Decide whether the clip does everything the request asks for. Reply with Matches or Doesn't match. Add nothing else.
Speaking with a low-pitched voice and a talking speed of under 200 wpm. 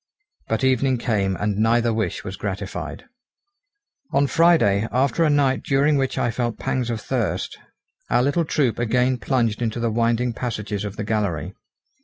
Matches